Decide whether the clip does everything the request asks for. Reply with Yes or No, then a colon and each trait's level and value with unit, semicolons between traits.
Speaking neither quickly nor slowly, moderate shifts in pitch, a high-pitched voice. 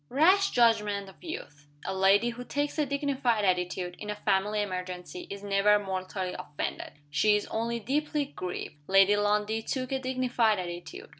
Yes: average, 160 wpm; average, 5.0 semitones; high, 210 Hz